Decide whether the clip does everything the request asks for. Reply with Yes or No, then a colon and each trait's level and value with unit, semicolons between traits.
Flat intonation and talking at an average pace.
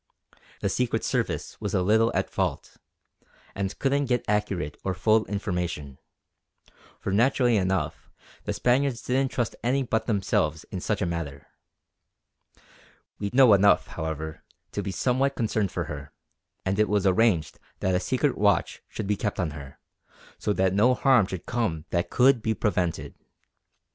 No: average, 5.0 semitones; average, 155 wpm